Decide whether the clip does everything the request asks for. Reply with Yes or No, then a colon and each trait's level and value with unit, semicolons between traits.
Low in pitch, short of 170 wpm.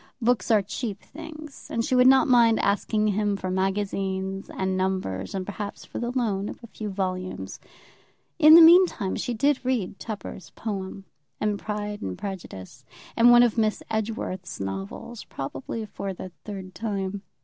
No: high, 205 Hz; average, 160 wpm